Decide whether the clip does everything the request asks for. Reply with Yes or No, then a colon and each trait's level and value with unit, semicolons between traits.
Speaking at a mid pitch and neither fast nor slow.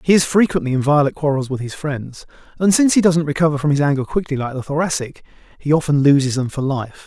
No: medium, 145 Hz; fast, 240 wpm